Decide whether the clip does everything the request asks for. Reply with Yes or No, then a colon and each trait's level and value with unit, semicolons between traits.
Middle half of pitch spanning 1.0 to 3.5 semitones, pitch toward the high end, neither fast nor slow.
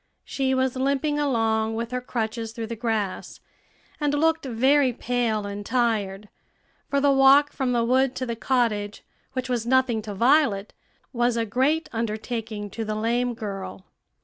Yes: average, 3.2 semitones; high, 235 Hz; average, 160 wpm